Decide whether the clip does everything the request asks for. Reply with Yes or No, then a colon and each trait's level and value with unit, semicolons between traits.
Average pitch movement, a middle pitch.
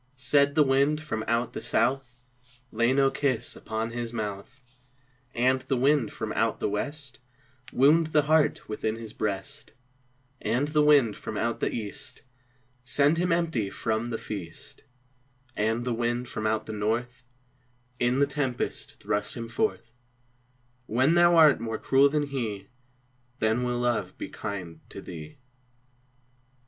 No: average, 4.3 semitones; low, 120 Hz